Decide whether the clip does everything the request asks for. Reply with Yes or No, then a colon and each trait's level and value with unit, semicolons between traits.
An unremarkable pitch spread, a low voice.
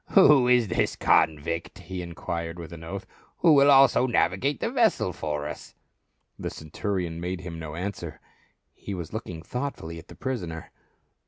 No: wide, 7.0 semitones; very low, 90 Hz